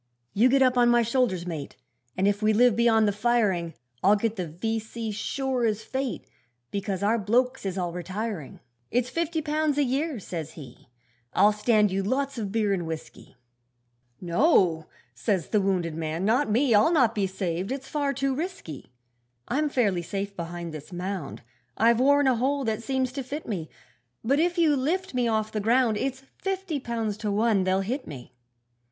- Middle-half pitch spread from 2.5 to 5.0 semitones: No, wide, 5.5 semitones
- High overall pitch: Yes, high, 220 Hz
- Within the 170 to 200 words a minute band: Yes, average, 185 wpm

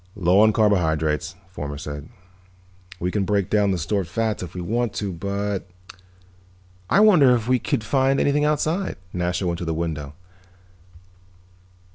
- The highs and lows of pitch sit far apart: No, average, 4.4 semitones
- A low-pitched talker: Yes, very low, 95 Hz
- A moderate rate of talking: Yes, average, 155 wpm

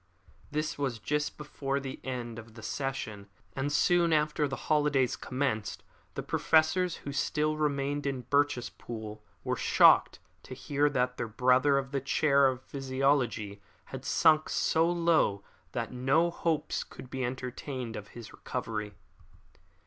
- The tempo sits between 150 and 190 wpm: No, average, 140 wpm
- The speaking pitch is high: No, low, 135 Hz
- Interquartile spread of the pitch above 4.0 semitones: No, average, 3.2 semitones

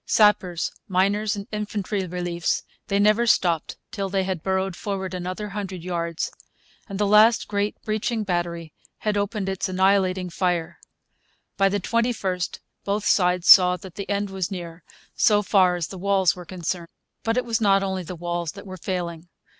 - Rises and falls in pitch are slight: Yes, narrow, 2.3 semitones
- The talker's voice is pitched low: No, high, 190 Hz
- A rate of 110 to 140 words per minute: No, average, 170 wpm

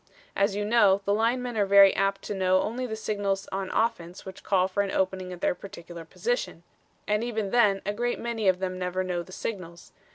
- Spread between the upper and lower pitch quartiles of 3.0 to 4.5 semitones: No, narrow, 2.6 semitones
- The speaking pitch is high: Yes, high, 195 Hz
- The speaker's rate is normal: No, fast, 215 wpm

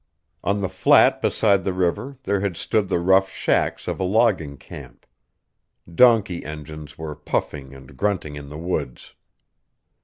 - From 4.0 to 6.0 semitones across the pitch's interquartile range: Yes, average, 4.9 semitones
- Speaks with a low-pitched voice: Yes, very low, 90 Hz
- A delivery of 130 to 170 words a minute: Yes, average, 150 wpm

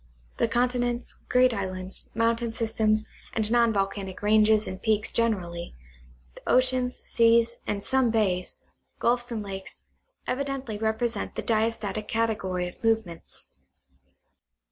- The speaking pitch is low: No, high, 220 Hz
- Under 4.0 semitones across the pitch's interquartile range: Yes, average, 2.9 semitones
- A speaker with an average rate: No, slow, 120 wpm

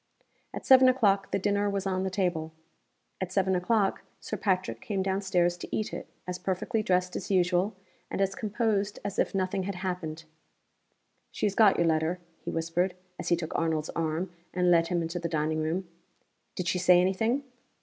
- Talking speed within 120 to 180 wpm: No, average, 190 wpm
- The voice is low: No, medium, 185 Hz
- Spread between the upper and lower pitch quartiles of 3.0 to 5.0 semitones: No, narrow, 2.5 semitones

